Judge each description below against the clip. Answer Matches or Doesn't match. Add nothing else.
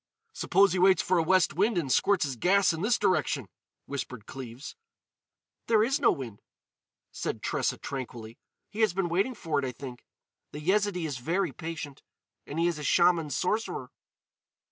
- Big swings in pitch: Matches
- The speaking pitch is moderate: Matches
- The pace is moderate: Matches